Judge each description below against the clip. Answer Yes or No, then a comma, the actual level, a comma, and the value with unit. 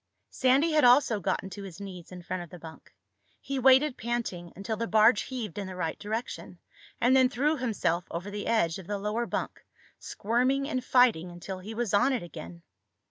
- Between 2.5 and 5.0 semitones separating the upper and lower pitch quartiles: No, wide, 5.5 semitones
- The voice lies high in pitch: Yes, high, 215 Hz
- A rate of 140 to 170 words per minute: No, average, 195 wpm